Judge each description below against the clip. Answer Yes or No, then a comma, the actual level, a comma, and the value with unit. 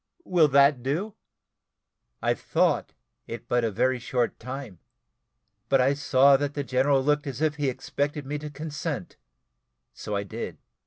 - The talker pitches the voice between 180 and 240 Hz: No, medium, 140 Hz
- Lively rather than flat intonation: No, narrow, 2.5 semitones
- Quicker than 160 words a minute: No, average, 155 wpm